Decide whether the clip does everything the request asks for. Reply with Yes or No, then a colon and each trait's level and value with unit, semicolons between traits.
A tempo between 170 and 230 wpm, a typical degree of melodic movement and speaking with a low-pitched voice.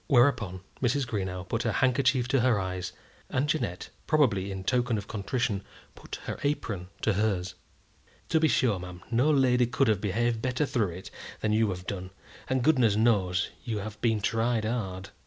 Yes: average, 175 wpm; average, 4.6 semitones; low, 110 Hz